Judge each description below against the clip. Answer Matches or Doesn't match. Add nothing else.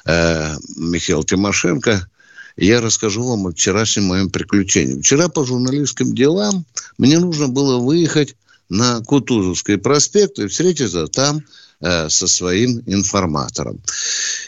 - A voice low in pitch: Matches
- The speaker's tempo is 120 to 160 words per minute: Doesn't match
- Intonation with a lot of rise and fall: Matches